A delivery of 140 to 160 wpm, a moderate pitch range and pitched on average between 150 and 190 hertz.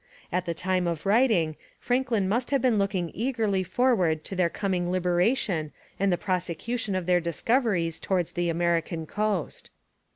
Yes: average, 155 wpm; average, 4.1 semitones; medium, 185 Hz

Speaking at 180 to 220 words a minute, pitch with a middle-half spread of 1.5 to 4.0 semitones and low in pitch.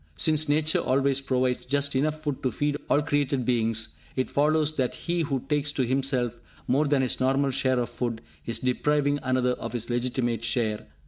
Yes: average, 185 wpm; average, 2.8 semitones; low, 130 Hz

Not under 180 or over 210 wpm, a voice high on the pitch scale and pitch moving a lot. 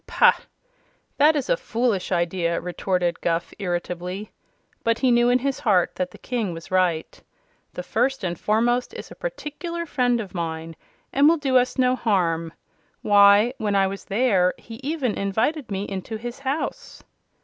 No: average, 165 wpm; high, 215 Hz; wide, 5.8 semitones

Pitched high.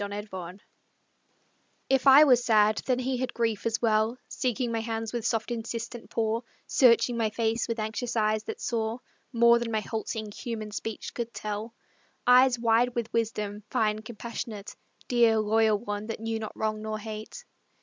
Yes: high, 225 Hz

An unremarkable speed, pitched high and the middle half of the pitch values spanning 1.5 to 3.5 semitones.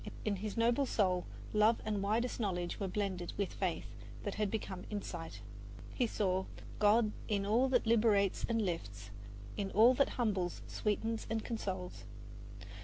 Yes: average, 150 wpm; high, 205 Hz; average, 3.1 semitones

